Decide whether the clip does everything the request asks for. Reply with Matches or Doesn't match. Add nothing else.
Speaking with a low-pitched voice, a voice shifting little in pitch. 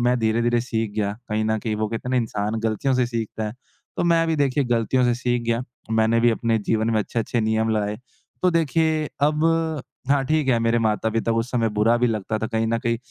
Matches